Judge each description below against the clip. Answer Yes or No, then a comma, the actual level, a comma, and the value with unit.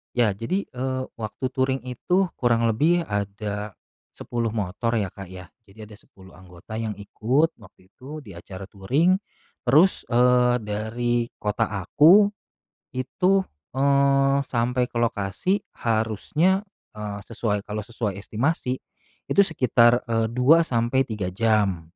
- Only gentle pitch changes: No, average, 4.3 semitones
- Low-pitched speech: Yes, low, 115 Hz